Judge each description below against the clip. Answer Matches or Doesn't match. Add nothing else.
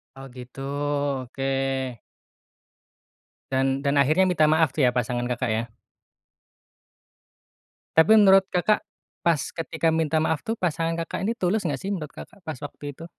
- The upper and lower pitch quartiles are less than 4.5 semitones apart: Doesn't match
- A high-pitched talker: Doesn't match